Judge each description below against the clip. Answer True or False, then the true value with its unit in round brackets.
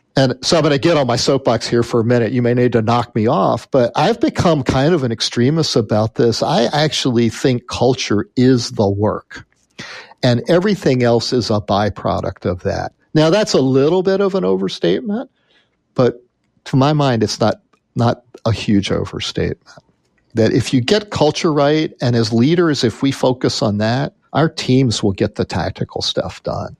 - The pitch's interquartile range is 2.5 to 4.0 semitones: False (4.5 semitones)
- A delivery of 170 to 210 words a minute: True (190 wpm)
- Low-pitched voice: True (125 Hz)